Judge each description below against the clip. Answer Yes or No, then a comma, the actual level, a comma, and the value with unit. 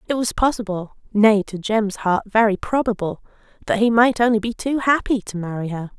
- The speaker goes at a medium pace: Yes, average, 190 wpm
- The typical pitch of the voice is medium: No, high, 215 Hz